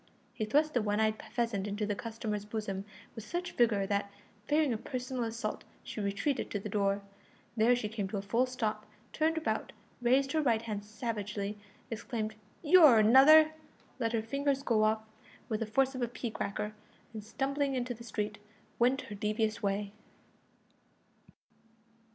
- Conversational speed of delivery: Yes, average, 165 wpm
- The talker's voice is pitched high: Yes, high, 225 Hz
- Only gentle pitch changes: No, average, 3.5 semitones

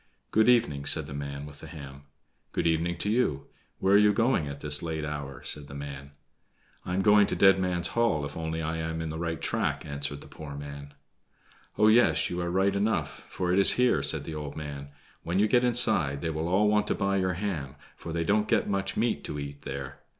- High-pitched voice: No, very low, 80 Hz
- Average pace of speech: No, fast, 230 wpm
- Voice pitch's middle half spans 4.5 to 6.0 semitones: Yes, wide, 5.5 semitones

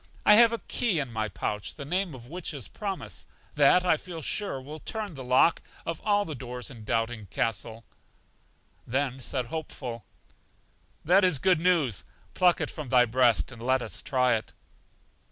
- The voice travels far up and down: Yes, wide, 6.7 semitones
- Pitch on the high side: No, low, 135 Hz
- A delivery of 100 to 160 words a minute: No, average, 175 wpm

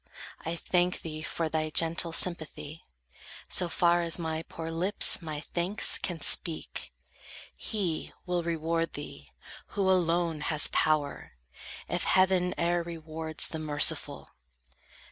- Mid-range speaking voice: Yes, medium, 165 Hz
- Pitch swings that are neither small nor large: No, narrow, 1.8 semitones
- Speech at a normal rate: No, slow, 125 wpm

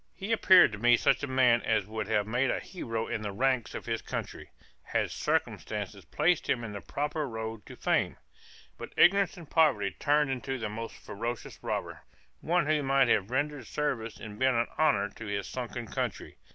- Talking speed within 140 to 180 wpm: No, average, 190 wpm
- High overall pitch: No, low, 125 Hz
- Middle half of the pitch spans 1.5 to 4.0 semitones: No, average, 4.9 semitones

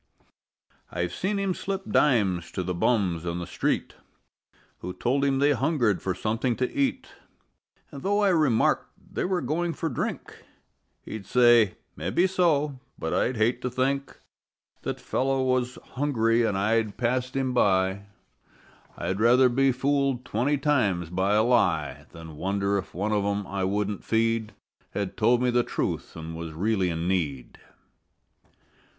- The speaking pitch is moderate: No, low, 115 Hz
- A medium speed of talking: Yes, average, 155 wpm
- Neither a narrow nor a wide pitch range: No, wide, 5.8 semitones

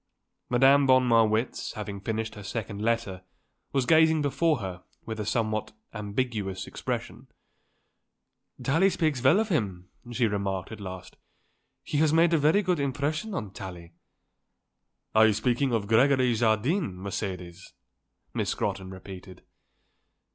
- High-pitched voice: No, low, 115 Hz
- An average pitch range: No, wide, 6.0 semitones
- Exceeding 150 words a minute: No, slow, 135 wpm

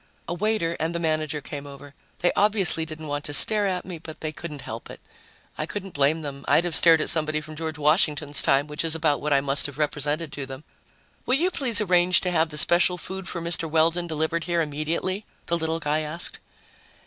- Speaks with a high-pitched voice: No, medium, 160 Hz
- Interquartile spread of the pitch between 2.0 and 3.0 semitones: Yes, average, 2.7 semitones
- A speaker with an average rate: No, fast, 220 wpm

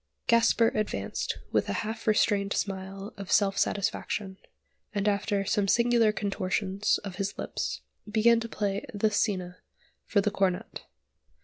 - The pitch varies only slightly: Yes, narrow, 1.7 semitones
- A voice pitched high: Yes, high, 205 Hz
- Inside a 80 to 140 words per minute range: Yes, slow, 135 wpm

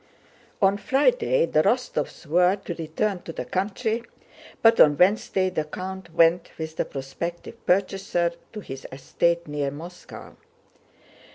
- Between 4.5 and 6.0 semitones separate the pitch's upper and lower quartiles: No, average, 3.5 semitones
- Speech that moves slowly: Yes, slow, 130 wpm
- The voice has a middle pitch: Yes, medium, 180 Hz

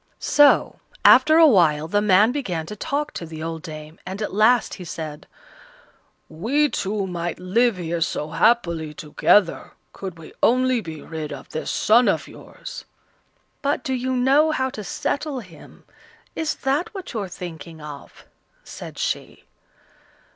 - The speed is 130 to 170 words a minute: Yes, average, 155 wpm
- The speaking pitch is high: Yes, high, 195 Hz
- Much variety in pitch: Yes, wide, 7.9 semitones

